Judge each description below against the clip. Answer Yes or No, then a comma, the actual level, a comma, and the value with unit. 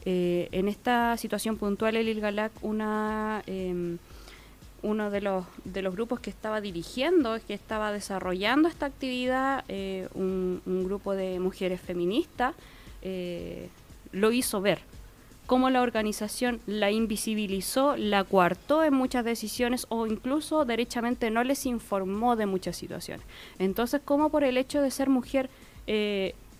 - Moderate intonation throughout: Yes, average, 4.6 semitones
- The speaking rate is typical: Yes, average, 140 wpm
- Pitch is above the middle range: Yes, high, 215 Hz